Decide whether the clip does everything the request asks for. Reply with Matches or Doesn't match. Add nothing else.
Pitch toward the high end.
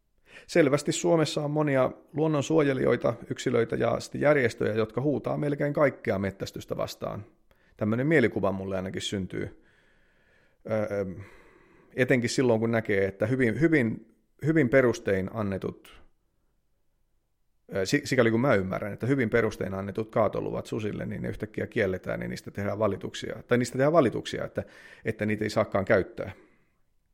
Doesn't match